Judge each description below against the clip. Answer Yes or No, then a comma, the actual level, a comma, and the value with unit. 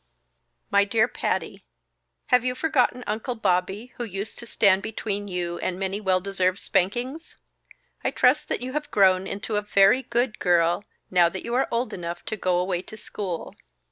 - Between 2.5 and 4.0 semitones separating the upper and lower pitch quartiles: No, average, 4.5 semitones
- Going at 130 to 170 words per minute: No, average, 180 wpm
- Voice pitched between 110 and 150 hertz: No, high, 200 Hz